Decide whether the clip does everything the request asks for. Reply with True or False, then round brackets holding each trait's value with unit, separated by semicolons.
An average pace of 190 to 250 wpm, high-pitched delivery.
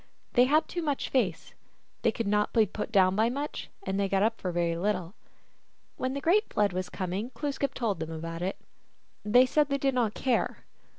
True (200 wpm; 210 Hz)